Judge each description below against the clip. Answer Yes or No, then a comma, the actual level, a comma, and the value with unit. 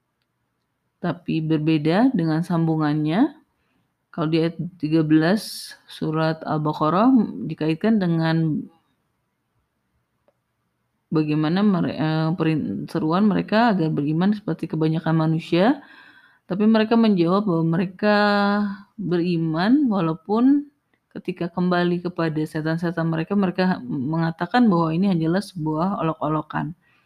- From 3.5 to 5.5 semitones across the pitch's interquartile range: Yes, average, 4.3 semitones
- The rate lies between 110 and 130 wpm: No, slow, 85 wpm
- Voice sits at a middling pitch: Yes, medium, 170 Hz